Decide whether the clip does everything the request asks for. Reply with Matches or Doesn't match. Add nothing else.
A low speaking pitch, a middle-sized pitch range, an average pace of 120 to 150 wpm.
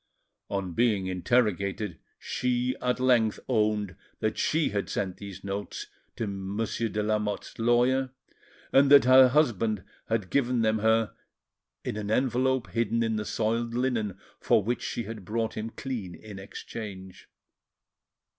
Matches